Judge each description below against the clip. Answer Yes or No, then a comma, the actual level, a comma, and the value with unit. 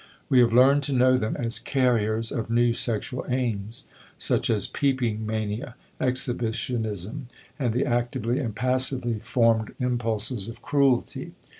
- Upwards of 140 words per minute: No, slow, 135 wpm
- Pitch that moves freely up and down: No, narrow, 2.4 semitones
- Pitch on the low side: Yes, low, 120 Hz